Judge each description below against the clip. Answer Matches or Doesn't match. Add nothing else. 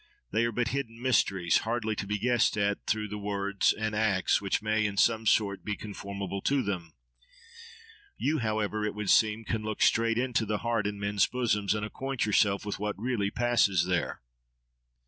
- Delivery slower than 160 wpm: Doesn't match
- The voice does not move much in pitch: Matches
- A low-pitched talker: Matches